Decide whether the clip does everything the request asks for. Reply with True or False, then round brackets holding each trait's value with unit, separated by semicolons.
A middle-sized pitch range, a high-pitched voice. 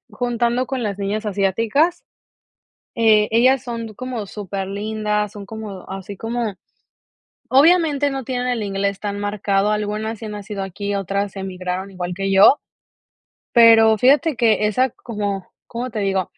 True (3.1 semitones; 210 Hz)